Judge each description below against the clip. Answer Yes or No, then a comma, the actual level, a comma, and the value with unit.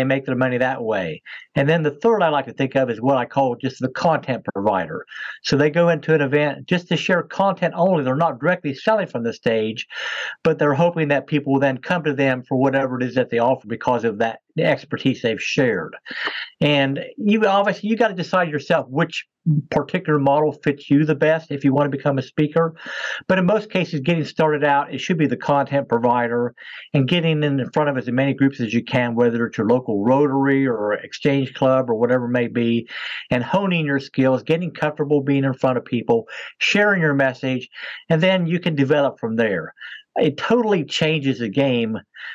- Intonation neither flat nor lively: Yes, average, 4.0 semitones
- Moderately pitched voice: Yes, medium, 145 Hz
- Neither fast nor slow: No, fast, 210 wpm